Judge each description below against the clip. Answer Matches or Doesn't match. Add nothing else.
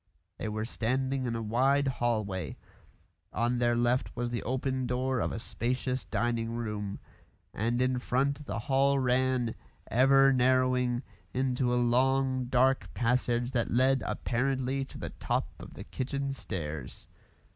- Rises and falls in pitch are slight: Matches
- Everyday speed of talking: Matches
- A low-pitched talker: Matches